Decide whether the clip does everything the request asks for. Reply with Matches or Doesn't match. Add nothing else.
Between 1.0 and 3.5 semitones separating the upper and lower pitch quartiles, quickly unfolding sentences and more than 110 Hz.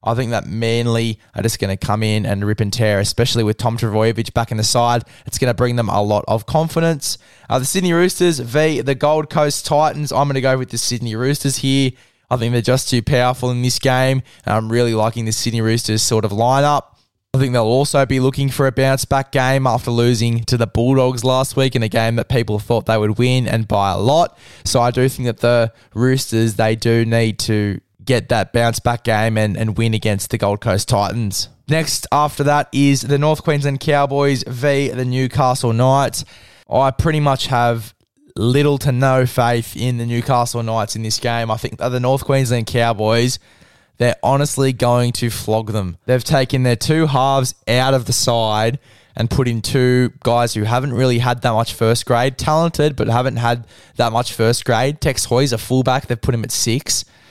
Matches